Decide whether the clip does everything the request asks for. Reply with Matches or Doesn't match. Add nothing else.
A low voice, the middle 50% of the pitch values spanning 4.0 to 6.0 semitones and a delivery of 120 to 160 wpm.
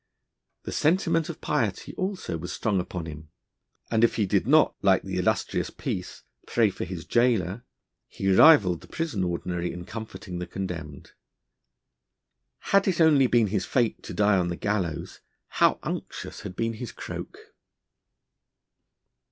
Matches